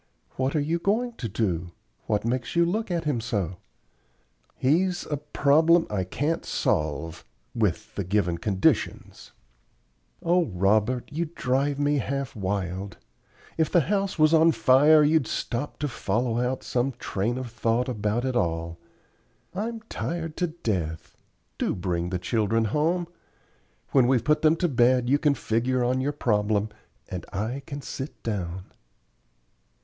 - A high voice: No, low, 125 Hz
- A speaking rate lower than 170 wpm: Yes, average, 150 wpm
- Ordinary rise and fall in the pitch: No, wide, 6.8 semitones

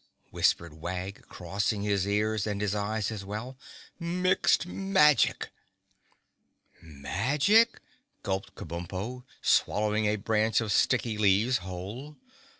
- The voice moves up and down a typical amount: Yes, average, 4.3 semitones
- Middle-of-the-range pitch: No, low, 105 Hz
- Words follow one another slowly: Yes, slow, 105 wpm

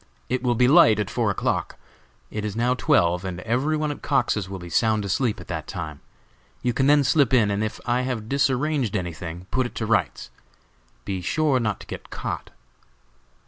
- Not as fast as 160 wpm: No, average, 195 wpm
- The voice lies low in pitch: Yes, low, 115 Hz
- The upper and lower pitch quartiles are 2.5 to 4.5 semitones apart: No, average, 5.2 semitones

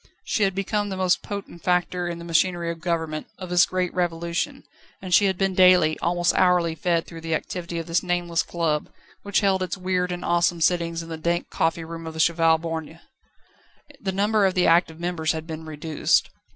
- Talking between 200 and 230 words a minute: Yes, fast, 205 wpm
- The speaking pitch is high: No, medium, 175 Hz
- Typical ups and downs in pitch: No, narrow, 1.8 semitones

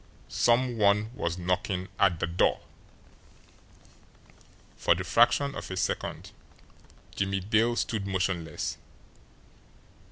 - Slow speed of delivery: Yes, slow, 100 wpm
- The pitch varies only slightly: No, average, 3.5 semitones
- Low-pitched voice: Yes, very low, 95 Hz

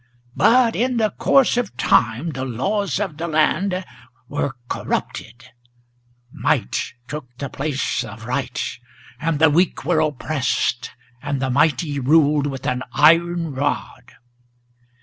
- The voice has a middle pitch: Yes, medium, 145 Hz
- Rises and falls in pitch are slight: No, average, 4.5 semitones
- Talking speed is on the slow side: Yes, slow, 130 wpm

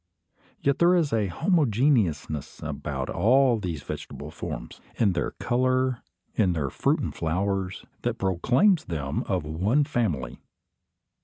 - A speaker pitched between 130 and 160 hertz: No, low, 105 Hz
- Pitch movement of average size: No, wide, 7.1 semitones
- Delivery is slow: Yes, slow, 130 wpm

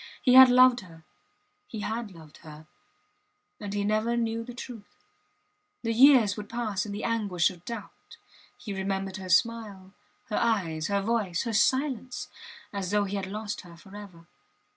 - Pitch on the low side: No, high, 205 Hz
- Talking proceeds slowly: No, average, 165 wpm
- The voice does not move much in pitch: No, average, 3.3 semitones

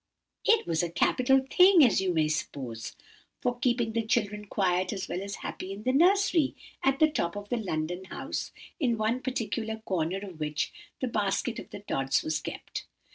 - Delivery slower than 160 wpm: No, average, 185 wpm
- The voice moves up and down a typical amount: No, wide, 5.9 semitones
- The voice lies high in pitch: Yes, high, 210 Hz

